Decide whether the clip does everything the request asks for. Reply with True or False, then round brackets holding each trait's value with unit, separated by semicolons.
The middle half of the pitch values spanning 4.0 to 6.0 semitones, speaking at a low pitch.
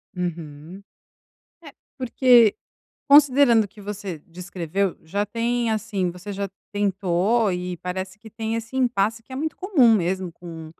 False (4.4 semitones; 205 Hz)